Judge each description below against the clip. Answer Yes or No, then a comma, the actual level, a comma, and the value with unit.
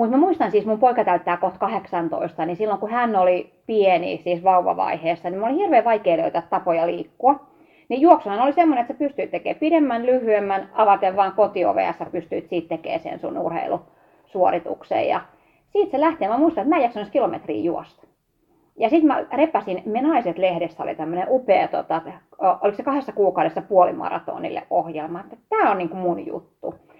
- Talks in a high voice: Yes, high, 210 Hz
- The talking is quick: Yes, fast, 170 wpm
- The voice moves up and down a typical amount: No, wide, 7.6 semitones